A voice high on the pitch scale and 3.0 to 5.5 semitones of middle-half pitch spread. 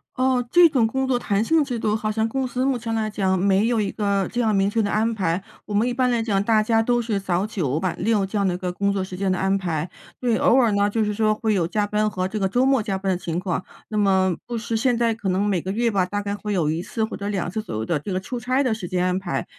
Yes: high, 210 Hz; average, 3.3 semitones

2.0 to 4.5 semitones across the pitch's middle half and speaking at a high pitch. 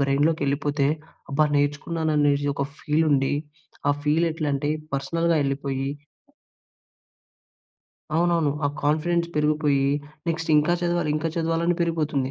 No: narrow, 2.6 semitones; medium, 150 Hz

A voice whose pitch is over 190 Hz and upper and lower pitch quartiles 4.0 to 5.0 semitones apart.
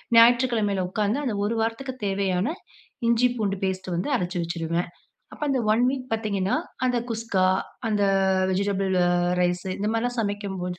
No: high, 205 Hz; average, 3.6 semitones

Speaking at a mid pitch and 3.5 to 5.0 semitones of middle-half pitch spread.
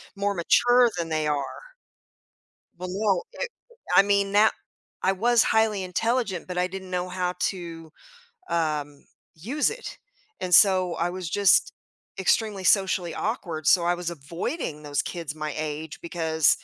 Yes: medium, 180 Hz; average, 3.8 semitones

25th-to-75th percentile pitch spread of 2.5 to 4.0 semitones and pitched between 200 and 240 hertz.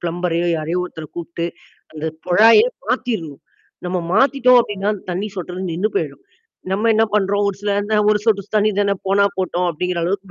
No: average, 3.2 semitones; high, 190 Hz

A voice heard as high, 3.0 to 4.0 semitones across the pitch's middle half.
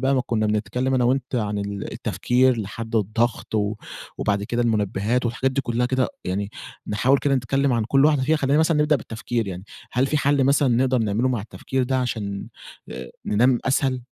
No: low, 120 Hz; average, 3.7 semitones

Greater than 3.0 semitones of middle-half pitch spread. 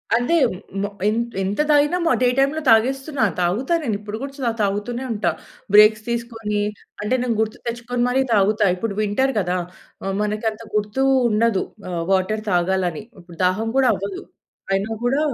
Yes: average, 3.4 semitones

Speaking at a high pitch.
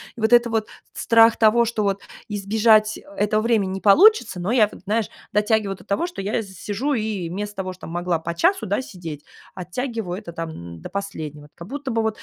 Yes: high, 210 Hz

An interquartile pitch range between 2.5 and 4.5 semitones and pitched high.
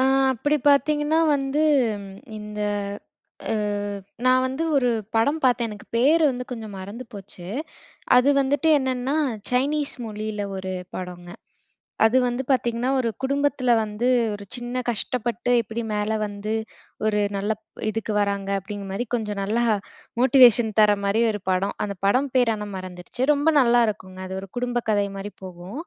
Yes: average, 3.9 semitones; high, 230 Hz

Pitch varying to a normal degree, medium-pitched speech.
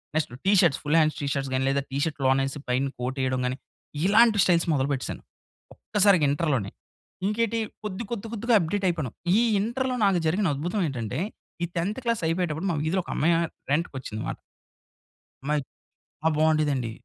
No: wide, 6.3 semitones; medium, 160 Hz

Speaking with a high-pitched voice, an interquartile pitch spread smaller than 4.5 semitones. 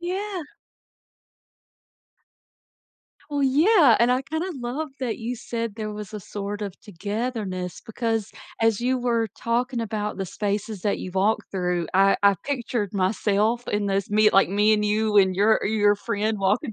Yes: high, 215 Hz; average, 3.1 semitones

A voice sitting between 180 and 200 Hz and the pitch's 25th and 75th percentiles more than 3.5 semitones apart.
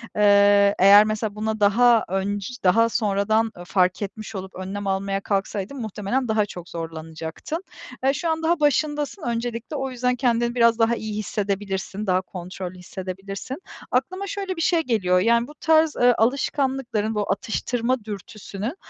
No: high, 215 Hz; average, 4.2 semitones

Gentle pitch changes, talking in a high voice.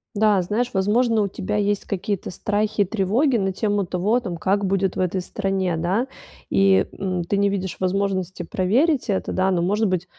Yes: narrow, 2.1 semitones; high, 195 Hz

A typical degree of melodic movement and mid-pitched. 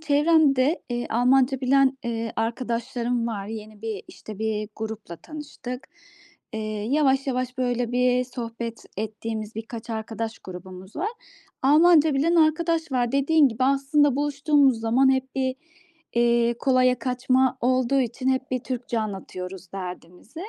No: average, 3.3 semitones; very high, 250 Hz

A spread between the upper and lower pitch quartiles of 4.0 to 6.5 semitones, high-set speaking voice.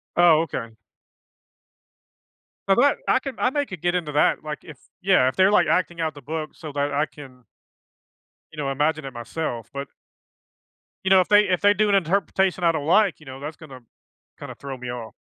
No: average, 5.1 semitones; medium, 160 Hz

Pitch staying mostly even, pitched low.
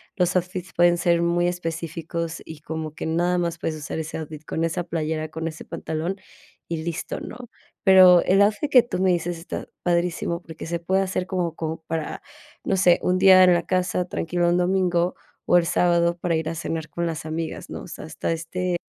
No: narrow, 1.8 semitones; medium, 170 Hz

